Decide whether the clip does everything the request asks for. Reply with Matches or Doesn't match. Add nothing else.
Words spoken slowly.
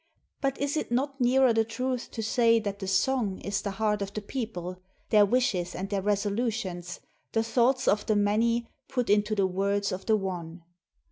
Doesn't match